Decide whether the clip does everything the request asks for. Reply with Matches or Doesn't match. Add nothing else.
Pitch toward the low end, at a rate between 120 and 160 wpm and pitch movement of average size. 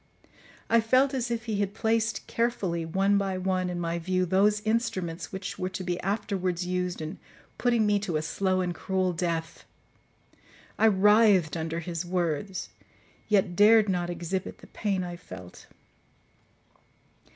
Doesn't match